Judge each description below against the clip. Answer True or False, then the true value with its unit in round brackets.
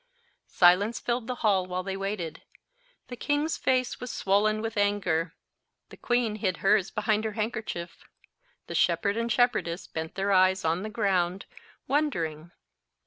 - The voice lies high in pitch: True (205 Hz)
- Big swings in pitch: False (3.8 semitones)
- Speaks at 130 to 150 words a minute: True (145 wpm)